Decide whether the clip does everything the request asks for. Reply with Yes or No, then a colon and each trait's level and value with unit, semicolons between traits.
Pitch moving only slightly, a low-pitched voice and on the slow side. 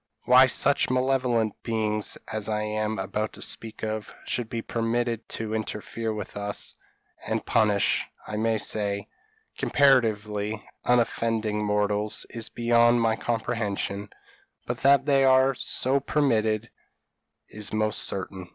Yes: narrow, 2.0 semitones; low, 110 Hz; slow, 125 wpm